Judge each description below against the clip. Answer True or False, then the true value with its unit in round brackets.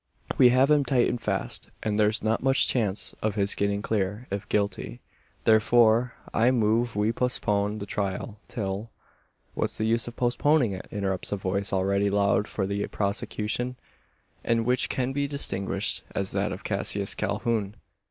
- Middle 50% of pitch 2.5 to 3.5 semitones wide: True (3.1 semitones)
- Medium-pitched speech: False (105 Hz)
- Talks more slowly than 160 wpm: False (165 wpm)